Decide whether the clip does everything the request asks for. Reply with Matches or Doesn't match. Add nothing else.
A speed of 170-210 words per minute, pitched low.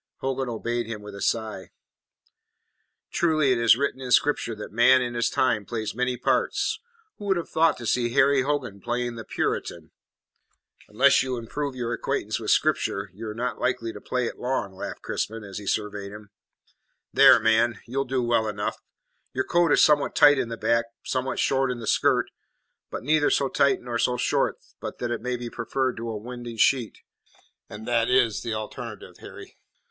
Matches